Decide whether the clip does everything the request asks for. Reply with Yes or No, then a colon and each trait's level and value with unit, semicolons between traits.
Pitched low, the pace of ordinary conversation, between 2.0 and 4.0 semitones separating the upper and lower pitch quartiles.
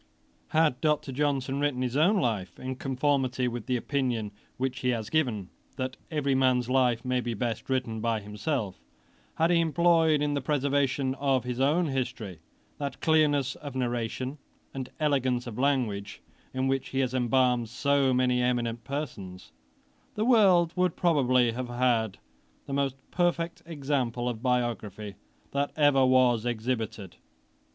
Yes: low, 130 Hz; average, 150 wpm; average, 2.9 semitones